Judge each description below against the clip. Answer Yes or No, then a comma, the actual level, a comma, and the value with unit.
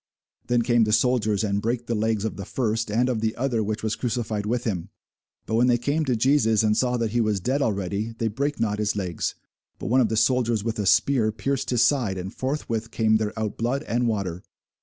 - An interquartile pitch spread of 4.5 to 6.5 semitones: No, narrow, 2.4 semitones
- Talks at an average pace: No, fast, 230 wpm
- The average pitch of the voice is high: No, low, 115 Hz